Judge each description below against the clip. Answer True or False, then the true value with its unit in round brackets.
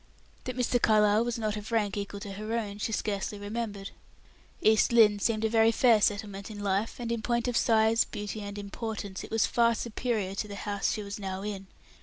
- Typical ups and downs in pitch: False (2.0 semitones)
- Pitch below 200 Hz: False (215 Hz)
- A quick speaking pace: True (210 wpm)